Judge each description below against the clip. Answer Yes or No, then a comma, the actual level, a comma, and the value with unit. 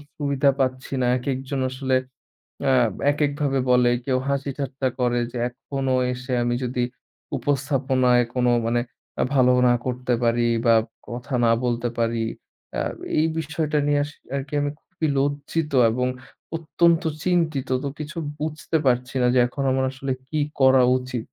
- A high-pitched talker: No, low, 130 Hz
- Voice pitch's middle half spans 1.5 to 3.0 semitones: Yes, narrow, 2.4 semitones